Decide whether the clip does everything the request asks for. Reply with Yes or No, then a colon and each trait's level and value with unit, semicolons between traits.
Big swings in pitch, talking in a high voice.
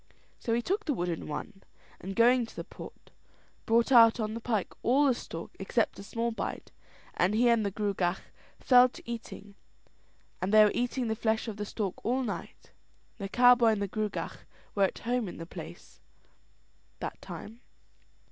No: average, 3.1 semitones; high, 220 Hz